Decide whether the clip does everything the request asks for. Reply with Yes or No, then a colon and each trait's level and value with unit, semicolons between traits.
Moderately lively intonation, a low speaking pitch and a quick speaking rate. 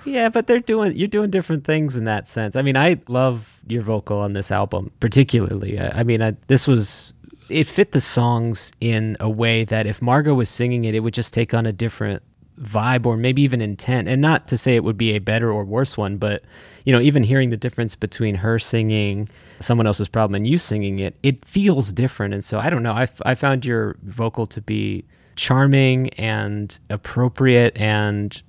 Yes: average, 3.7 semitones; low, 115 Hz; fast, 215 wpm